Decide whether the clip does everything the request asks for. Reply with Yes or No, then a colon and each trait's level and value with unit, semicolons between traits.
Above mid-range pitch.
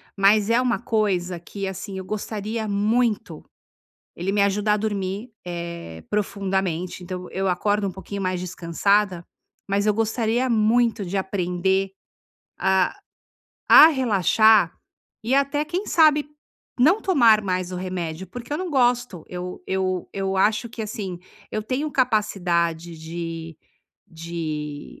Yes: high, 195 Hz